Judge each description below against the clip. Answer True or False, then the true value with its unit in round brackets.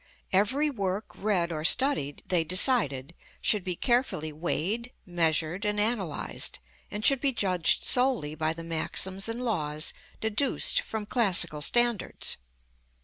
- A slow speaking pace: True (130 wpm)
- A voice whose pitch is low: False (195 Hz)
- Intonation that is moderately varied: False (6.4 semitones)